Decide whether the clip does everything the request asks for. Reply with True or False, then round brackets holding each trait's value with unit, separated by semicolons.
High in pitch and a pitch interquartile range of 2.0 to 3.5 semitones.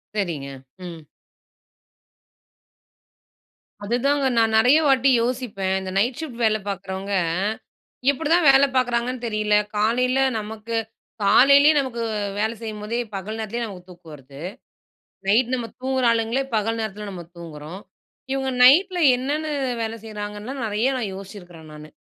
False (225 Hz; 4.3 semitones)